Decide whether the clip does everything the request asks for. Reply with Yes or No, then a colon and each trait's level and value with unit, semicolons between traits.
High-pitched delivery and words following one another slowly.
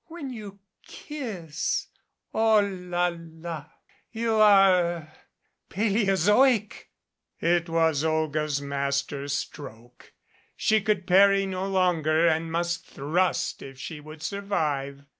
No: medium, 175 Hz; slow, 110 wpm